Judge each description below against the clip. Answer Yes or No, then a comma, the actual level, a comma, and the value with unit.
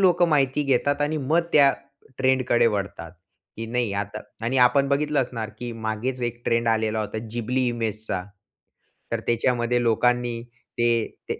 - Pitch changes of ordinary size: Yes, average, 3.0 semitones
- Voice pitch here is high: No, low, 120 Hz